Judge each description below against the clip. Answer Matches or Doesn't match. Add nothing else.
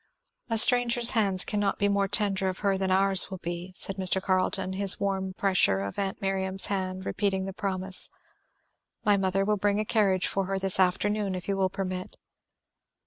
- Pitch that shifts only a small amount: Matches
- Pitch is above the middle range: Matches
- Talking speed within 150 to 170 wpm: Doesn't match